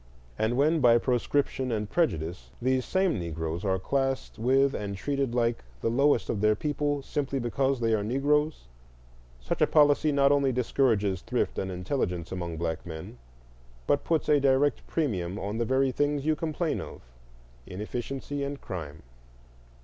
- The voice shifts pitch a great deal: Yes, wide, 6.9 semitones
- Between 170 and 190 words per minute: No, average, 155 wpm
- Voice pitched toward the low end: Yes, low, 125 Hz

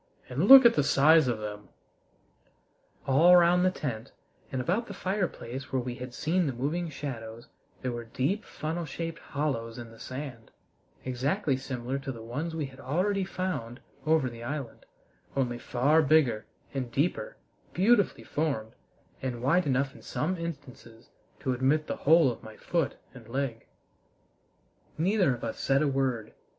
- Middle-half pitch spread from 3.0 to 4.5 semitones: No, average, 5.2 semitones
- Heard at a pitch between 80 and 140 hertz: Yes, low, 135 Hz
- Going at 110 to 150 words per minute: No, average, 160 wpm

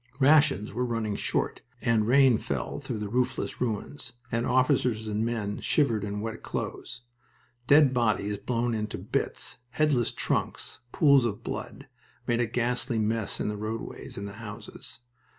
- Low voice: Yes, low, 115 Hz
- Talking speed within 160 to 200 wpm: No, average, 150 wpm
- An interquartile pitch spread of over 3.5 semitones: No, average, 2.8 semitones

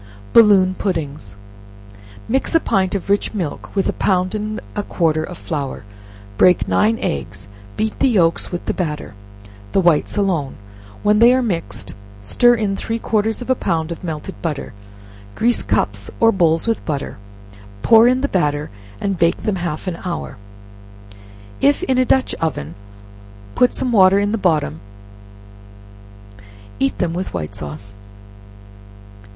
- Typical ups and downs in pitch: No, wide, 5.7 semitones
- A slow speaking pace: No, average, 150 wpm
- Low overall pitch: No, medium, 185 Hz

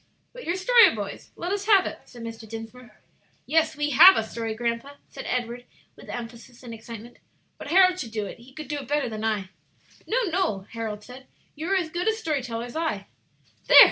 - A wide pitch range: Yes, wide, 6.2 semitones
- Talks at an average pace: No, fast, 210 wpm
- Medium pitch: No, very high, 250 Hz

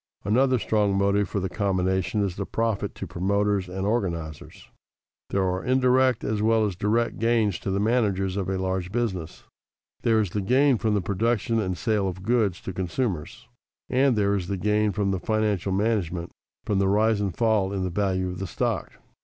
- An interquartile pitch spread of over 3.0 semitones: No, average, 2.7 semitones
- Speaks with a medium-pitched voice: No, low, 100 Hz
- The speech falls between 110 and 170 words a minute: No, average, 185 wpm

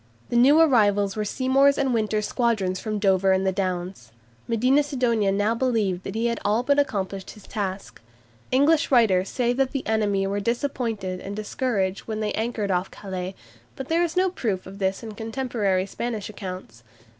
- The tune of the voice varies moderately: Yes, average, 4.2 semitones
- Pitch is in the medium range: No, high, 215 Hz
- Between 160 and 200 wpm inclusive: Yes, average, 180 wpm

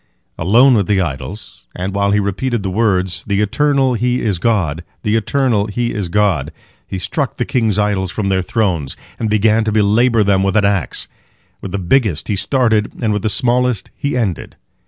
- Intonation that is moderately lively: Yes, average, 3.4 semitones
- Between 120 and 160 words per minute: No, average, 190 wpm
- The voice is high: No, low, 105 Hz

